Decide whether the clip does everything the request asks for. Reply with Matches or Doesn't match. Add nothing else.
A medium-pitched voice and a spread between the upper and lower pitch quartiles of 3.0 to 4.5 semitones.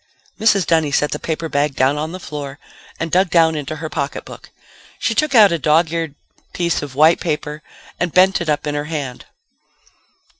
Doesn't match